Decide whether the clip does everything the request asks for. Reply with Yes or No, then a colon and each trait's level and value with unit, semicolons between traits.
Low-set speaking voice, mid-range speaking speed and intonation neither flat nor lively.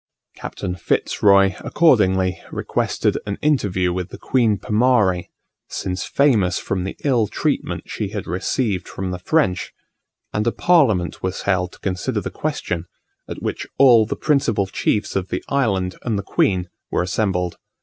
Yes: low, 100 Hz; average, 155 wpm; average, 3.9 semitones